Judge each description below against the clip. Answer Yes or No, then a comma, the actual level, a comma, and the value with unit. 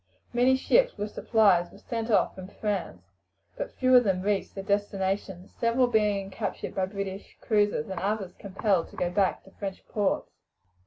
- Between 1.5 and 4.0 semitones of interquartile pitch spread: Yes, narrow, 2.4 semitones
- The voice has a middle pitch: No, high, 200 Hz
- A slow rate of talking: No, average, 170 wpm